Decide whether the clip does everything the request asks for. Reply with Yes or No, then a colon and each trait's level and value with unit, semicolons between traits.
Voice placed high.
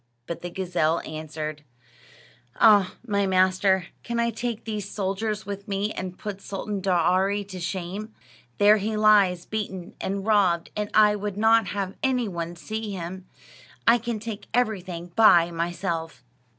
Yes: high, 195 Hz